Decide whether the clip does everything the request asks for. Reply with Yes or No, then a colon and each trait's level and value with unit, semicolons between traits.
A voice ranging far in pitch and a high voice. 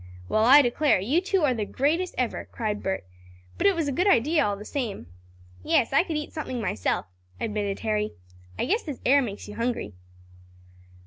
Yes: wide, 6.3 semitones; very high, 250 Hz